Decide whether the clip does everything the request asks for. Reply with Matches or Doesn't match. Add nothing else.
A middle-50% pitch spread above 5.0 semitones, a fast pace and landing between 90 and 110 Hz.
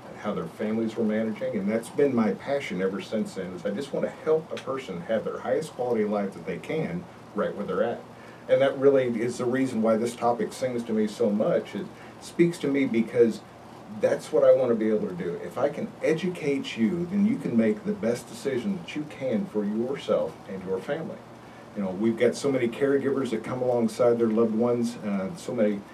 Doesn't match